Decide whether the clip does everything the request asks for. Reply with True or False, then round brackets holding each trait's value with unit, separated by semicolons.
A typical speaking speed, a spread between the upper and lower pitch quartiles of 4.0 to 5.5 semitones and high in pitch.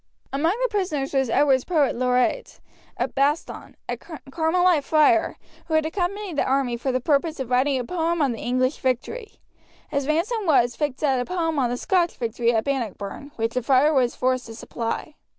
True (185 wpm; 4.4 semitones; 280 Hz)